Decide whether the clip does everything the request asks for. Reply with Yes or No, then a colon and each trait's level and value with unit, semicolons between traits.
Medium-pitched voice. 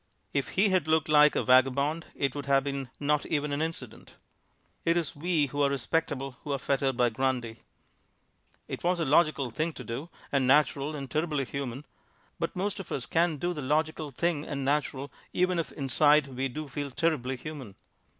Yes: medium, 145 Hz